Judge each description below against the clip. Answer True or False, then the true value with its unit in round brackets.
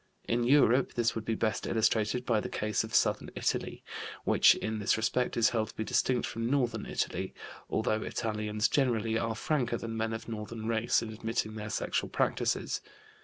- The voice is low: True (115 Hz)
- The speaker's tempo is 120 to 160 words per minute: False (180 wpm)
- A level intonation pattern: True (1.4 semitones)